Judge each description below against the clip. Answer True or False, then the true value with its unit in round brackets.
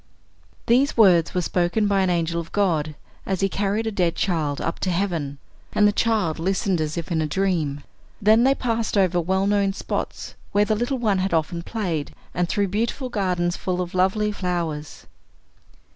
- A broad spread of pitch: False (3.5 semitones)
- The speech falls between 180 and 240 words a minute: True (185 wpm)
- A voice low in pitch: False (185 Hz)